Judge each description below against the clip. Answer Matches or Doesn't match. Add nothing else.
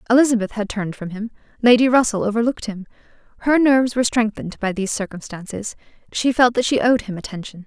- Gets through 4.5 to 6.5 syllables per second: Doesn't match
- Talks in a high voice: Matches